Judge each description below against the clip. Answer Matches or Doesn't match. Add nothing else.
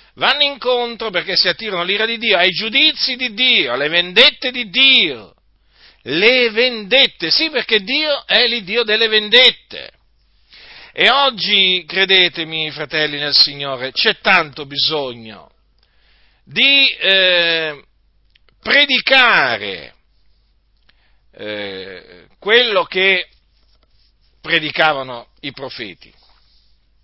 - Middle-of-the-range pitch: Doesn't match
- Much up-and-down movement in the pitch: Matches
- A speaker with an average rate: Doesn't match